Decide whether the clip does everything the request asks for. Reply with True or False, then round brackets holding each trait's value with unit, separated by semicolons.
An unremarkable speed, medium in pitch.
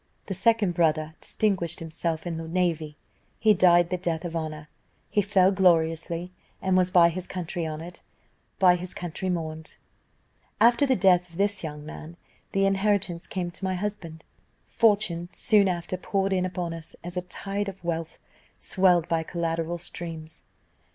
True (160 wpm; 175 Hz)